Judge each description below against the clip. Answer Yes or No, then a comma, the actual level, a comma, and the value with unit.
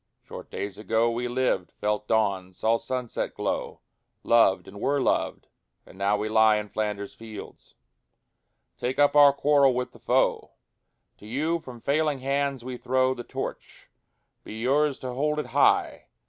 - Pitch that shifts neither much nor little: Yes, average, 4.4 semitones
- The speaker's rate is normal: Yes, average, 160 wpm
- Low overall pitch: Yes, low, 120 Hz